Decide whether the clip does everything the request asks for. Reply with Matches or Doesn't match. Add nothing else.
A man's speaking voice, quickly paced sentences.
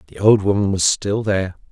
Matches